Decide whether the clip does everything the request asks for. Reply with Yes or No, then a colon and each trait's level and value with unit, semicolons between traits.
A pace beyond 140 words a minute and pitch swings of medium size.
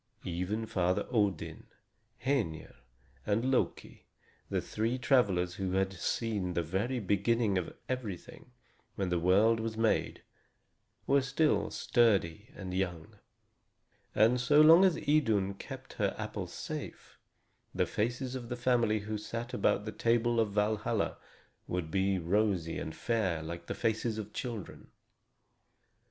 No: slow, 135 wpm; average, 4.2 semitones